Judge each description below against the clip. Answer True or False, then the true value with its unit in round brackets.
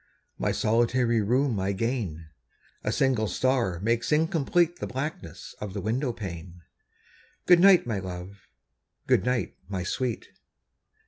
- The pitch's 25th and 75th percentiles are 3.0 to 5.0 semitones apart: False (5.4 semitones)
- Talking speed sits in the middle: False (130 wpm)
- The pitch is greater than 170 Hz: False (115 Hz)